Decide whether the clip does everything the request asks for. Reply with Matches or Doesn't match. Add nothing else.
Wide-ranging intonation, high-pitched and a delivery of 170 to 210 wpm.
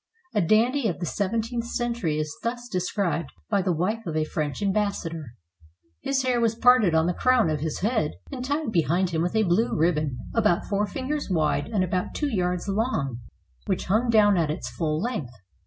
Matches